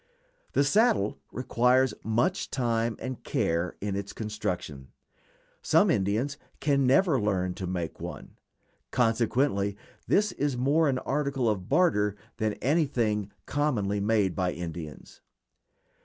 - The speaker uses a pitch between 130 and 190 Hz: No, low, 115 Hz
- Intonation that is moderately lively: No, wide, 5.7 semitones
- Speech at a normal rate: No, slow, 120 wpm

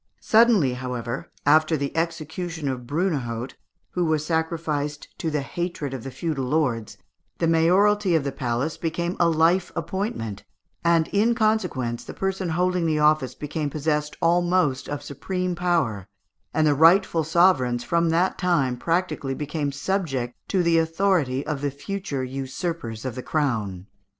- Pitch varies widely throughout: No, average, 4.5 semitones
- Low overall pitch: No, medium, 155 Hz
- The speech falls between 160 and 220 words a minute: No, average, 150 wpm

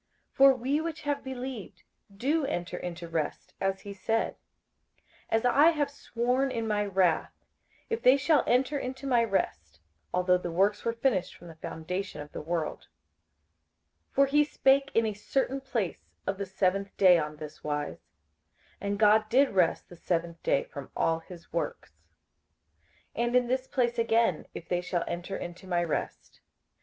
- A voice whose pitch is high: Yes, high, 210 Hz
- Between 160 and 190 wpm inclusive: Yes, average, 170 wpm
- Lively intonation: Yes, wide, 6.9 semitones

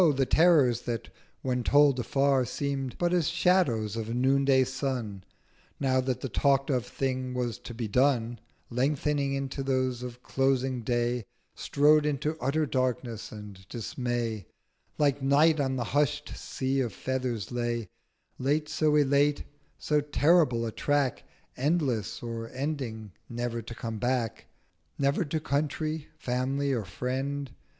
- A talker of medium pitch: No, low, 130 Hz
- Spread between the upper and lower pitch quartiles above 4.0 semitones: No, average, 3.0 semitones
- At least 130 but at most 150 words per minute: Yes, average, 140 wpm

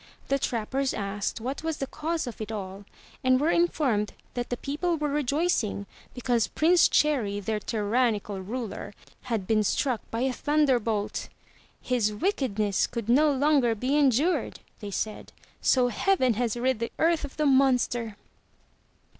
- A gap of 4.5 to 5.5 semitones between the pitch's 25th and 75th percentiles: Yes, average, 5.1 semitones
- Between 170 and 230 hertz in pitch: No, very high, 250 Hz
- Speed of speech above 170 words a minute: No, average, 150 wpm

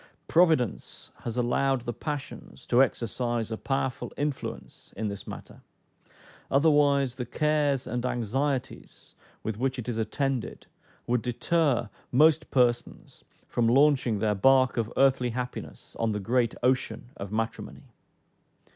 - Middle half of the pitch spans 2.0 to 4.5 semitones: Yes, average, 2.9 semitones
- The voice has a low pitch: Yes, low, 125 Hz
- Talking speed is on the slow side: Yes, slow, 130 wpm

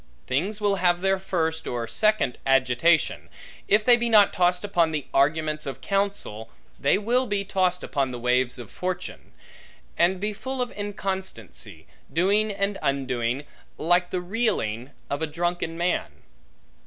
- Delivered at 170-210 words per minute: No, average, 150 wpm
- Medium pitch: Yes, medium, 175 Hz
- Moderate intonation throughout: No, wide, 6.2 semitones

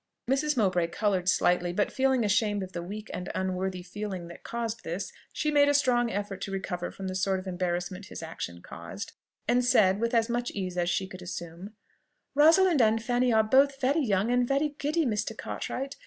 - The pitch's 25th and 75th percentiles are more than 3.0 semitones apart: Yes, average, 5.2 semitones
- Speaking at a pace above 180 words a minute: Yes, average, 200 wpm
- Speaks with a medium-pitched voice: No, high, 205 Hz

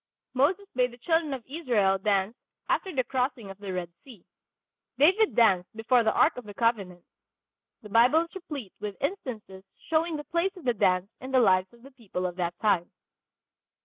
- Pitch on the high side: Yes, high, 235 Hz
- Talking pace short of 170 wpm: No, average, 185 wpm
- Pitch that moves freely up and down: Yes, wide, 6.6 semitones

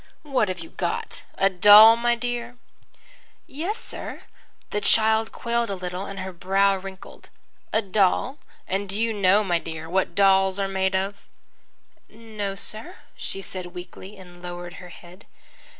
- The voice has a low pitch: No, high, 195 Hz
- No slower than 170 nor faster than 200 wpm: No, average, 155 wpm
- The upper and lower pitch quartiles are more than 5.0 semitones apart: No, average, 2.9 semitones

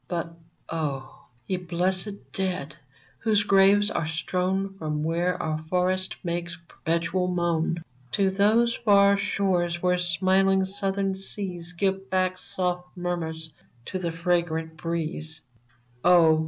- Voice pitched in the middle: Yes, medium, 180 Hz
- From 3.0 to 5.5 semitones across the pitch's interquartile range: No, narrow, 2.5 semitones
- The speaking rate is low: Yes, slow, 125 wpm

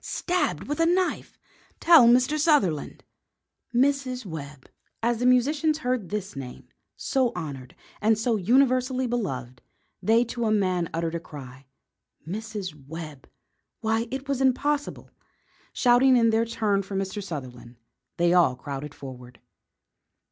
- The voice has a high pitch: Yes, high, 220 Hz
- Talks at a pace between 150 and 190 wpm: No, slow, 135 wpm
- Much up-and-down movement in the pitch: Yes, wide, 7.9 semitones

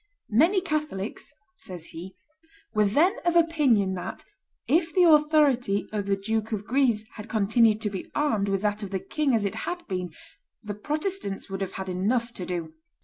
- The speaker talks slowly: No, average, 180 wpm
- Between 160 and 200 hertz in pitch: No, high, 220 Hz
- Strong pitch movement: Yes, wide, 7.3 semitones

